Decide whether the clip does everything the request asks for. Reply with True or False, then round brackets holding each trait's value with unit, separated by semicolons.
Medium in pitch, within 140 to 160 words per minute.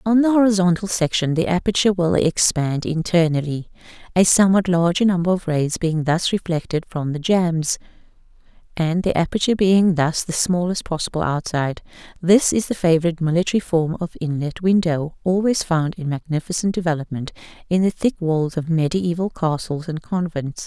True (170 Hz; 155 wpm)